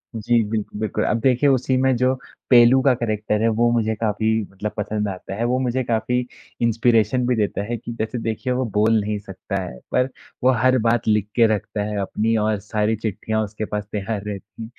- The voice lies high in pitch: No, low, 110 Hz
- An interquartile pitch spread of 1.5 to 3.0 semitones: Yes, narrow, 2.4 semitones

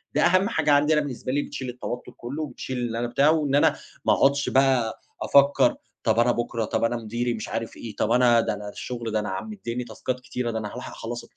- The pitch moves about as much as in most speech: Yes, average, 3.3 semitones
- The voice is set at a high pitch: No, low, 125 Hz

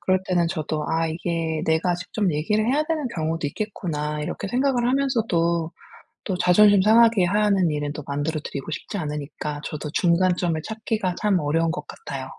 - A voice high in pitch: No, medium, 175 Hz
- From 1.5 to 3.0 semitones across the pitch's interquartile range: No, average, 5.2 semitones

